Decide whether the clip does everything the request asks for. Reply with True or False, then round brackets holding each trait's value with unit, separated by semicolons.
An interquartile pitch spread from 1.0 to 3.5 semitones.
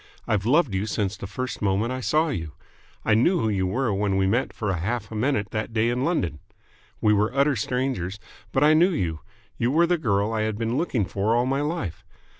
False (5.1 semitones)